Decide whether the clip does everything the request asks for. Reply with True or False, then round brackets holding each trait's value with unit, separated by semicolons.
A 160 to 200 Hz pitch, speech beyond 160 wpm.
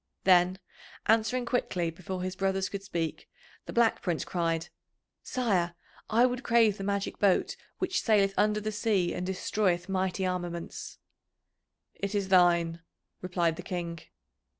False (190 Hz; 140 wpm)